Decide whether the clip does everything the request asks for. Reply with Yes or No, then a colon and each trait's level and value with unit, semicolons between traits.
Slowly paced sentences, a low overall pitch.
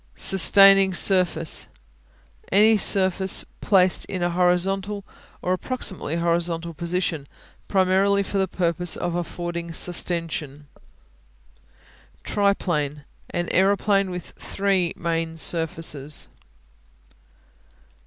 No: slow, 85 wpm; medium, 180 Hz